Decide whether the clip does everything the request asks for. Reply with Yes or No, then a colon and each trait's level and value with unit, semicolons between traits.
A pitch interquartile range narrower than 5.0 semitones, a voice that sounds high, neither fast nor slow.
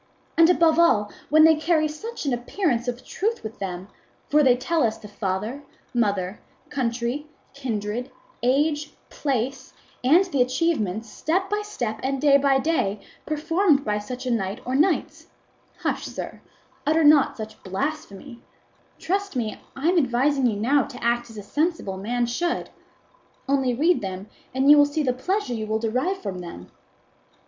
No: wide, 5.6 semitones; very high, 260 Hz; average, 165 wpm